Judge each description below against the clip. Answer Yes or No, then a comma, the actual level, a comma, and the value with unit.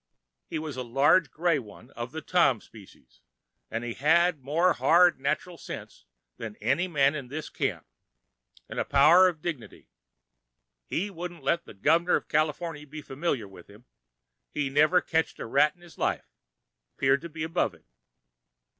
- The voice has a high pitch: No, medium, 150 Hz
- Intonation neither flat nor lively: No, wide, 5.7 semitones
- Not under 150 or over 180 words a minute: Yes, average, 160 wpm